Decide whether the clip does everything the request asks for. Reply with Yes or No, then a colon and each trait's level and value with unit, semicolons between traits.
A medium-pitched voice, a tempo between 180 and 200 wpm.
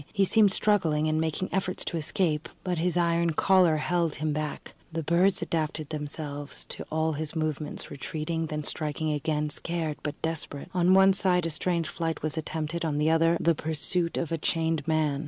Yes: medium, 160 Hz; average, 185 wpm